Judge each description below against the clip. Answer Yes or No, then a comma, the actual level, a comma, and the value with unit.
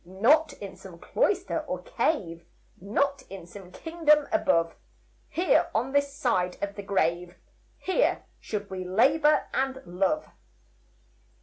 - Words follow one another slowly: Yes, slow, 125 wpm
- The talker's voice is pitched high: Yes, high, 220 Hz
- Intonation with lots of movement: Yes, wide, 8.3 semitones